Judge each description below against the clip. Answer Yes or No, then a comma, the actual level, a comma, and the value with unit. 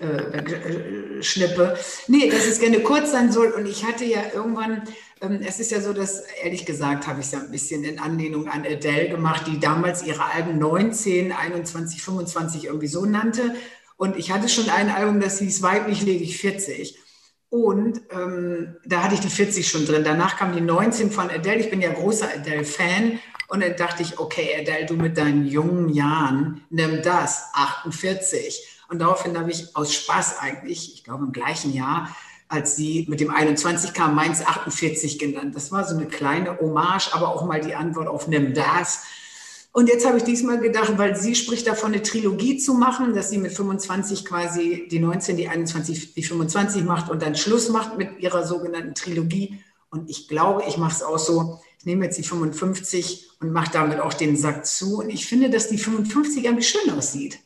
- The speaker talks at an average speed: No, fast, 195 wpm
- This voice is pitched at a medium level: Yes, medium, 175 Hz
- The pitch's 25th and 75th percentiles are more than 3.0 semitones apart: Yes, average, 4.6 semitones